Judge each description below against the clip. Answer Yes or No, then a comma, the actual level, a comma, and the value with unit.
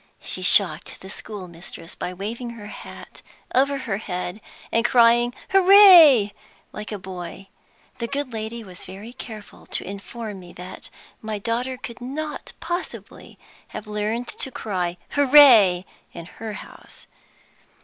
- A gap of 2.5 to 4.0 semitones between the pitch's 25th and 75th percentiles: No, average, 4.6 semitones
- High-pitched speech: Yes, high, 220 Hz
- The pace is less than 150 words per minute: Yes, slow, 135 wpm